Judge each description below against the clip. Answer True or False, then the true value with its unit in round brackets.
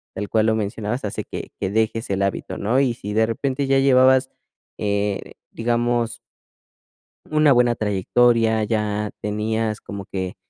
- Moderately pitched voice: False (110 Hz)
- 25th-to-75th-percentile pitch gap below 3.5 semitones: True (2.8 semitones)